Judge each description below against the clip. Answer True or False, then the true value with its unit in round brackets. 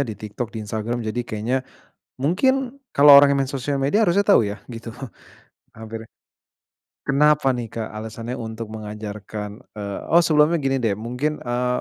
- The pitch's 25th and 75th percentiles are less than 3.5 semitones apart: False (4.6 semitones)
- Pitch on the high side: False (120 Hz)